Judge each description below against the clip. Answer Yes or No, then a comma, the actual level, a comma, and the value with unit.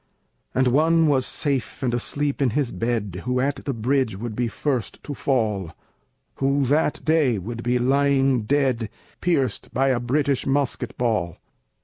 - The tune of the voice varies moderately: Yes, average, 3.1 semitones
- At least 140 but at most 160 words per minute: Yes, average, 155 wpm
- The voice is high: No, low, 130 Hz